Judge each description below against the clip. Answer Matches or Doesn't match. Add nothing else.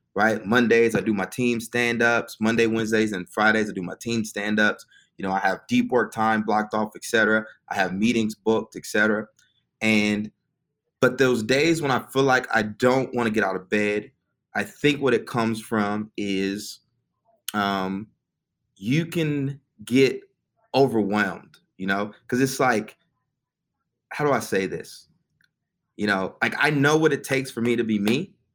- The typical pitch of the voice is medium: Doesn't match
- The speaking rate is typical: Matches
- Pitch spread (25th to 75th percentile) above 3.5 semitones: Matches